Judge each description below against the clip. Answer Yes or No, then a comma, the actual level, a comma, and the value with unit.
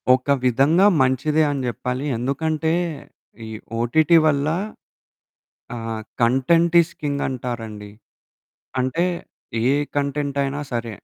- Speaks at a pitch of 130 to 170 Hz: Yes, medium, 140 Hz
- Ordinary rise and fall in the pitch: Yes, average, 4.1 semitones